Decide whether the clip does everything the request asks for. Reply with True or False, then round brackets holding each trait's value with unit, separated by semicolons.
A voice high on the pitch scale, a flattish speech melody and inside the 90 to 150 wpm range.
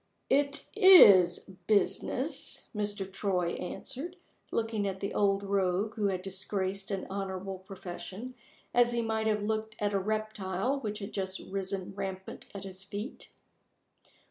True (200 Hz; 2.3 semitones; 140 wpm)